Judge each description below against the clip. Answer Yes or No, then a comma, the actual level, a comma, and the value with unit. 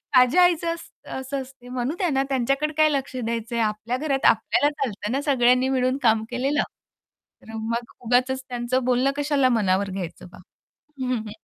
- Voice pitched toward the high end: Yes, very high, 255 Hz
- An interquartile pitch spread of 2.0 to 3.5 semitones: Yes, average, 2.8 semitones